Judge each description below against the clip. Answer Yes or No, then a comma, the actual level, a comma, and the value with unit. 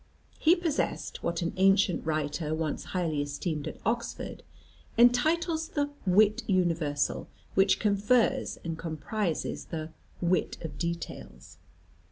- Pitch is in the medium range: Yes, medium, 180 Hz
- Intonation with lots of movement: Yes, wide, 5.7 semitones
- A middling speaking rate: No, slow, 115 wpm